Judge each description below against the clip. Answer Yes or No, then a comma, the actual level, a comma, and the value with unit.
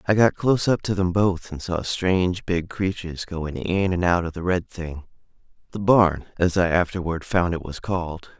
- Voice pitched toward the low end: Yes, very low, 90 Hz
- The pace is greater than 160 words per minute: Yes, average, 200 wpm